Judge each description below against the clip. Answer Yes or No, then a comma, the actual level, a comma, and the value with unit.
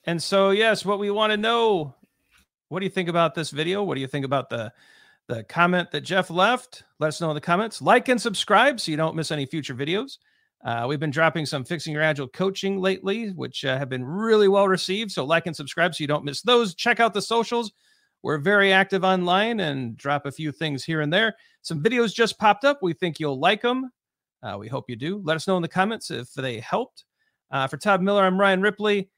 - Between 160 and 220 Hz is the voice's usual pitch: Yes, medium, 185 Hz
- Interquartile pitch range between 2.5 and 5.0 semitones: No, wide, 5.6 semitones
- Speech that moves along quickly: Yes, fast, 235 wpm